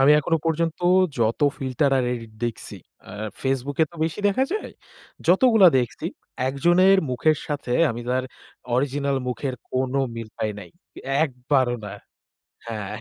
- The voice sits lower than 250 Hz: Yes, low, 135 Hz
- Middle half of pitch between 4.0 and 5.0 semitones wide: Yes, average, 4.7 semitones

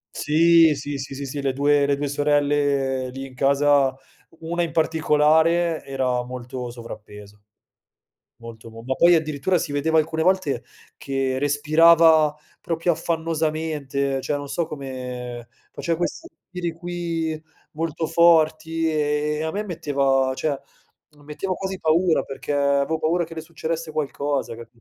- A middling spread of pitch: Yes, average, 3.1 semitones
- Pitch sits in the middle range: Yes, medium, 150 Hz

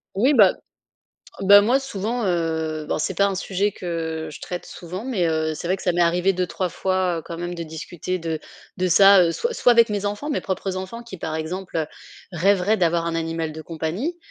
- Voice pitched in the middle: Yes, medium, 180 Hz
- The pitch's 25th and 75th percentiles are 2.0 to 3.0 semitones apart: No, average, 3.4 semitones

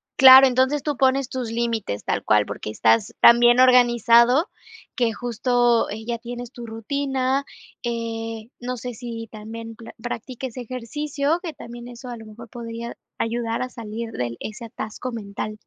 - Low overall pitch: No, high, 235 Hz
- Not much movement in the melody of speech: Yes, narrow, 2.0 semitones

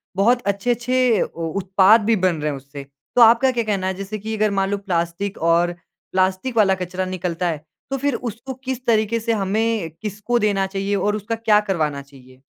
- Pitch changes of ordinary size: Yes, average, 3.6 semitones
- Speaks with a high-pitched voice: Yes, high, 200 Hz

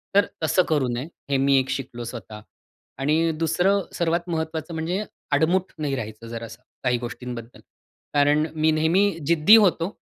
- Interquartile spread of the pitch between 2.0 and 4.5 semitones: No, average, 4.9 semitones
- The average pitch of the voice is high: No, medium, 155 Hz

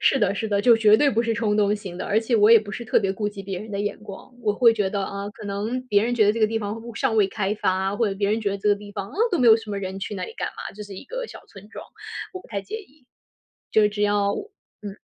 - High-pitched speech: Yes, high, 210 Hz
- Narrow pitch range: Yes, narrow, 2.1 semitones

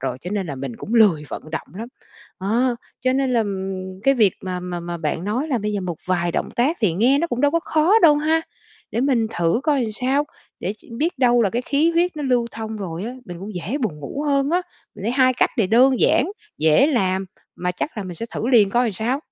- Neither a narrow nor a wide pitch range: No, wide, 6.6 semitones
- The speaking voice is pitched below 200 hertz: No, high, 225 Hz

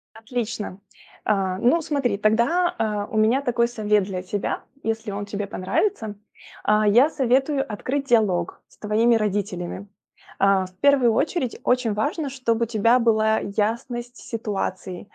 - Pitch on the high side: Yes, high, 220 Hz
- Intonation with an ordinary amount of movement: Yes, average, 3.3 semitones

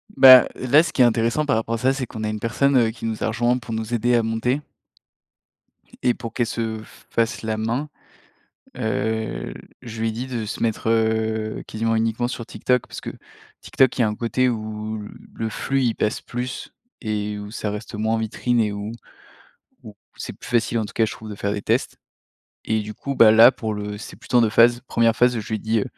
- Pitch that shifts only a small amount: Yes, narrow, 1.9 semitones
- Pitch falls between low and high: No, low, 115 Hz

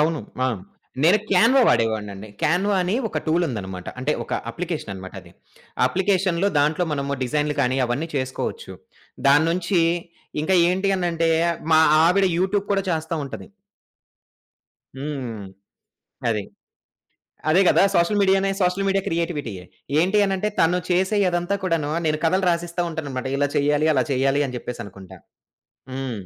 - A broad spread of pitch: Yes, wide, 5.7 semitones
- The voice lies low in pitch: No, medium, 160 Hz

